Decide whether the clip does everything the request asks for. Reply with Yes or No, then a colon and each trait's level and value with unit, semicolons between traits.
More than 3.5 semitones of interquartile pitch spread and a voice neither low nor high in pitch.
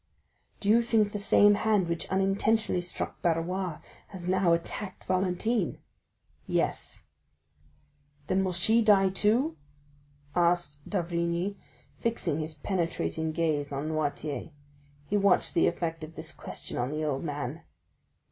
Yes: average, 3.9 semitones; medium, 175 Hz